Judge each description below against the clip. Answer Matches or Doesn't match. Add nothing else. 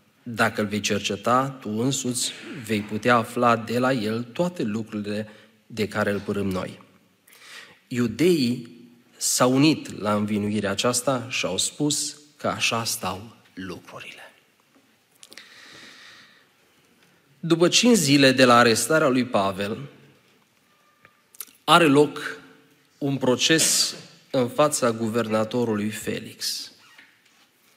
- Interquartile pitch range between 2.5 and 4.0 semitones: Doesn't match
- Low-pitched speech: Matches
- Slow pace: Matches